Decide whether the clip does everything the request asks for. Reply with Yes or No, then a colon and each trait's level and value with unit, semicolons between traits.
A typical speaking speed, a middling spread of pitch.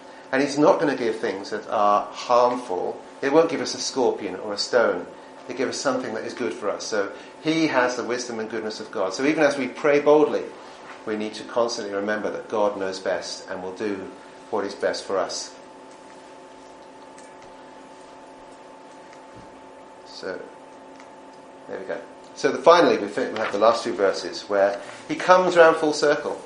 No: average, 180 wpm; wide, 6.6 semitones